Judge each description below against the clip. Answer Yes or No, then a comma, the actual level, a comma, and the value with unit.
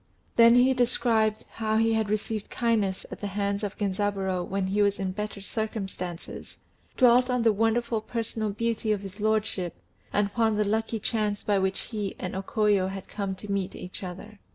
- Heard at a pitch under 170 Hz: No, high, 210 Hz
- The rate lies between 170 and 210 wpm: Yes, average, 185 wpm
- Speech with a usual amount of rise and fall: No, narrow, 2.2 semitones